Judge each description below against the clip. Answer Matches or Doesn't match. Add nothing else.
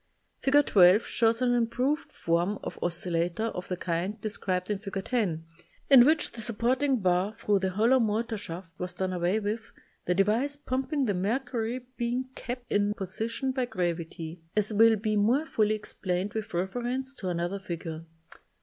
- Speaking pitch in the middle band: Doesn't match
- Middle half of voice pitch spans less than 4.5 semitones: Doesn't match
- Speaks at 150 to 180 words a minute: Matches